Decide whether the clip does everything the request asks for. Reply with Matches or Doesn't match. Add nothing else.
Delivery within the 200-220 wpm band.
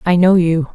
Doesn't match